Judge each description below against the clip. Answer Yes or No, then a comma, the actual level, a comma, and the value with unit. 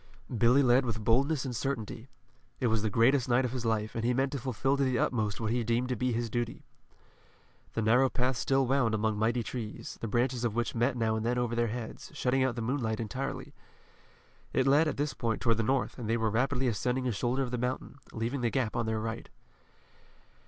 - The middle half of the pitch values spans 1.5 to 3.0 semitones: Yes, narrow, 2.5 semitones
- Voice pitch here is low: Yes, low, 120 Hz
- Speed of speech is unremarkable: No, fast, 225 wpm